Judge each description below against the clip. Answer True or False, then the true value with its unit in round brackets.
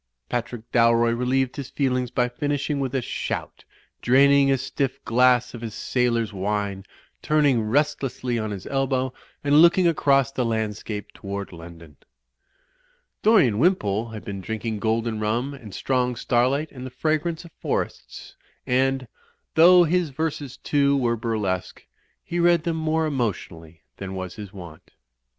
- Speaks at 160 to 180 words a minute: False (145 wpm)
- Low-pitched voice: True (125 Hz)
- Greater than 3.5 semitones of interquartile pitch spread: True (4.5 semitones)